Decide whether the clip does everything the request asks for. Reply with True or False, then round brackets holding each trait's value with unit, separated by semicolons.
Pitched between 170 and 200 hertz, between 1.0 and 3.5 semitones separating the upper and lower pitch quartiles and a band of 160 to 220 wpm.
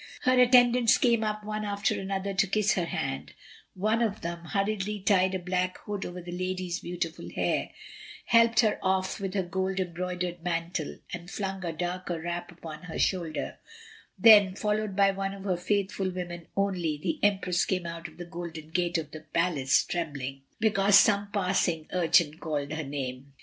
True (185 Hz; 2.9 semitones; 175 wpm)